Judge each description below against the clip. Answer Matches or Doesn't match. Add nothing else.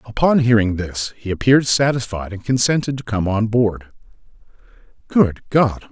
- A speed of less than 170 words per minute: Matches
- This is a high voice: Doesn't match